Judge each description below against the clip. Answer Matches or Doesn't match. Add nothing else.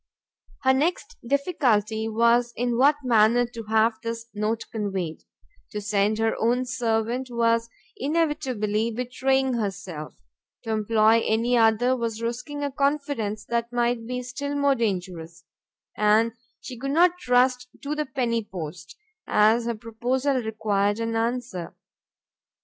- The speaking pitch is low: Doesn't match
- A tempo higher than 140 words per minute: Doesn't match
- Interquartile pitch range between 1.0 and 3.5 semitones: Matches